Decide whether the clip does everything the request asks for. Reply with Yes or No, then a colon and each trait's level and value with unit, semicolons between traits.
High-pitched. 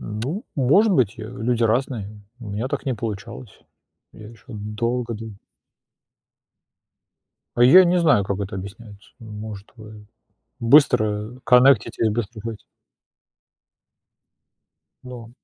No: low, 115 Hz